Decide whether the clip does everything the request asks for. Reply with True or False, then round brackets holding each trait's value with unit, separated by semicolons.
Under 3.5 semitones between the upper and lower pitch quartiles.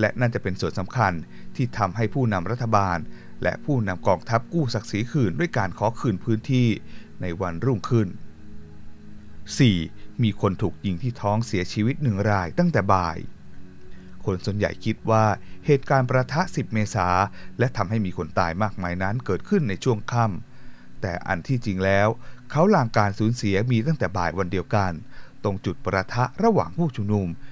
False (4.8 semitones)